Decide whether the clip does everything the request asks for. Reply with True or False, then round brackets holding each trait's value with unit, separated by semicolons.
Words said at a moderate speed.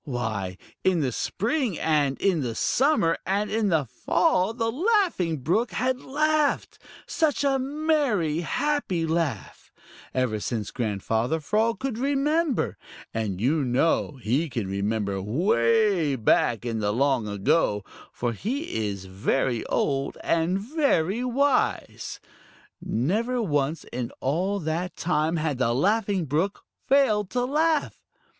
False (130 wpm)